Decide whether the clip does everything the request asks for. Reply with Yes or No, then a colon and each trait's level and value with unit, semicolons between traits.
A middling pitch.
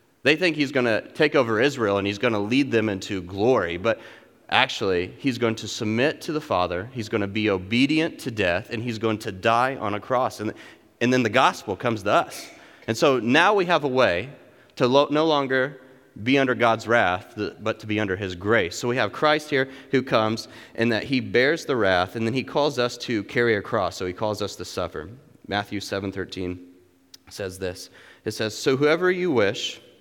No: low, 115 Hz